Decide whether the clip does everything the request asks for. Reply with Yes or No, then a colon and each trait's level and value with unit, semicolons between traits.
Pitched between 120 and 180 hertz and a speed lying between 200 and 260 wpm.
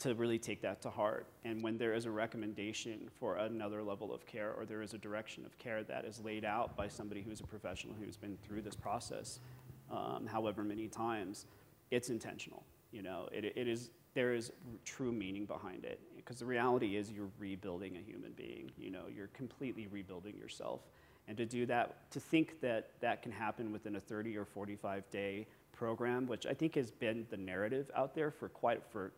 No: low, 110 Hz; fast, 205 wpm